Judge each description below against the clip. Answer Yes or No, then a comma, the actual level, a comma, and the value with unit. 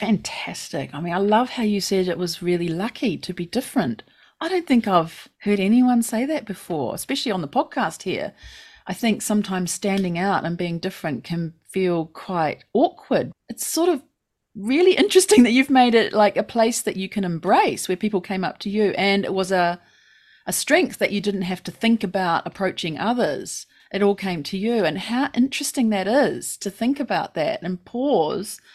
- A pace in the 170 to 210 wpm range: Yes, average, 195 wpm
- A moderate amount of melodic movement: Yes, average, 4.8 semitones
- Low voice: No, high, 205 Hz